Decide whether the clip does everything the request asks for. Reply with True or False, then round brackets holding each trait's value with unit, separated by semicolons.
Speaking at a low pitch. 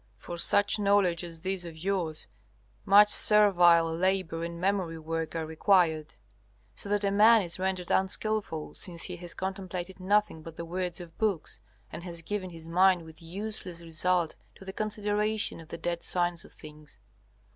False (180 Hz)